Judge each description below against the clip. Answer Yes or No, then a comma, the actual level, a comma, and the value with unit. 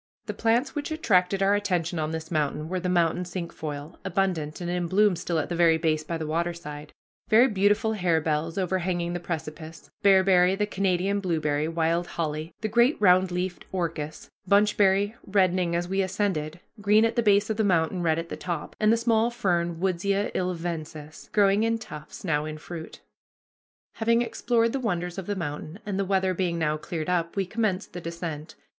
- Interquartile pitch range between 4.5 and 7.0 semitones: No, average, 3.5 semitones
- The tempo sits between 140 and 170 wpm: No, average, 185 wpm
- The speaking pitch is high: No, medium, 180 Hz